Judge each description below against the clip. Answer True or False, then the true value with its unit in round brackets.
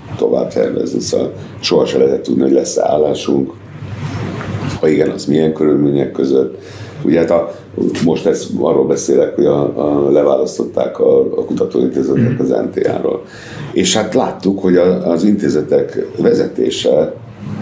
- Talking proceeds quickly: False (135 wpm)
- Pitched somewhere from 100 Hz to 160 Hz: True (105 Hz)